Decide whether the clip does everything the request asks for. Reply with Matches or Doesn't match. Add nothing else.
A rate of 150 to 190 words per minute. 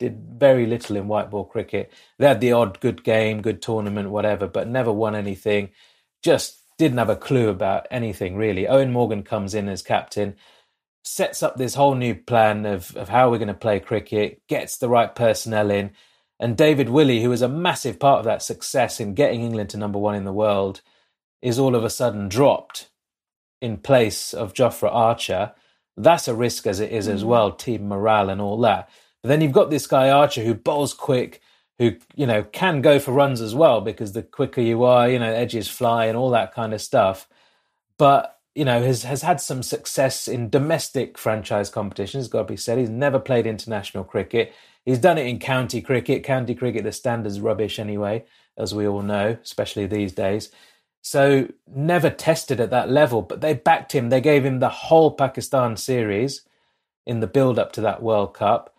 Doesn't match